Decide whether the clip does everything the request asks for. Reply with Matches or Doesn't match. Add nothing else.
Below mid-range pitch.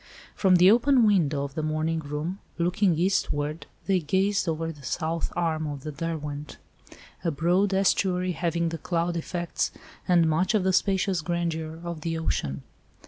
Doesn't match